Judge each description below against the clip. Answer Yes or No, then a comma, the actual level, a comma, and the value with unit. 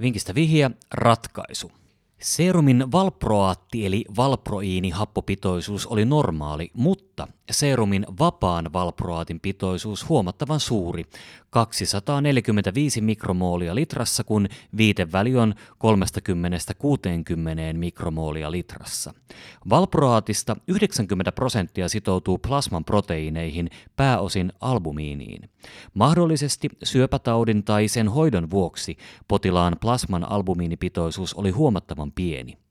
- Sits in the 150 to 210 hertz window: No, low, 105 Hz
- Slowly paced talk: Yes, slow, 85 wpm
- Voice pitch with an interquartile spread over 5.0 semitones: Yes, wide, 5.6 semitones